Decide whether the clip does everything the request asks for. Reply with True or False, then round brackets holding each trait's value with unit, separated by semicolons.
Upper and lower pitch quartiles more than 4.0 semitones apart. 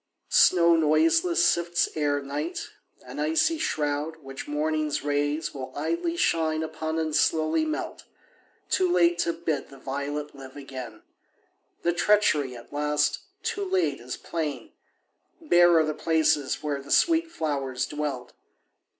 False (3.1 semitones)